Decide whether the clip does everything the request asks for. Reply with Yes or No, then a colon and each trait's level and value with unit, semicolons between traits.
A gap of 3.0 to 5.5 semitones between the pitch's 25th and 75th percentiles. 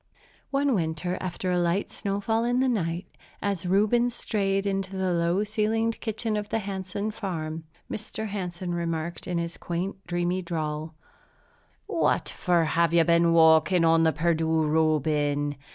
Yes: average, 3.7 semitones